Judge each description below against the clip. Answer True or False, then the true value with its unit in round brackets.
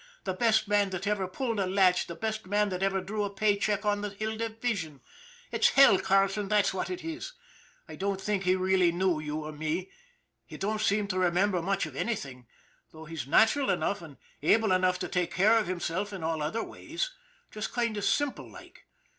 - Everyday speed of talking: False (210 wpm)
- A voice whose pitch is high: True (195 Hz)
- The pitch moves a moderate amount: True (3.1 semitones)